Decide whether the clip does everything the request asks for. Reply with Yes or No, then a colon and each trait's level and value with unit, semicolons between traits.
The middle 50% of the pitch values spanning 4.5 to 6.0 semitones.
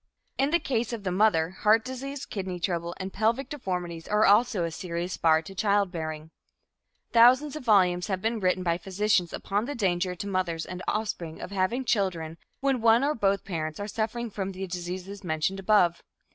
No: average, 4.0 semitones